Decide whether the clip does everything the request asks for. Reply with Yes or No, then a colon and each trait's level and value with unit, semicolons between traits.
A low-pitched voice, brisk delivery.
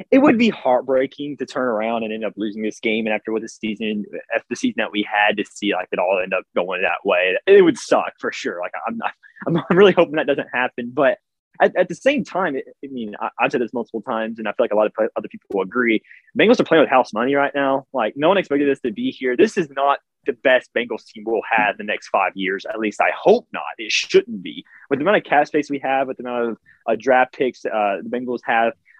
Yes: low, 130 Hz; fast, 275 wpm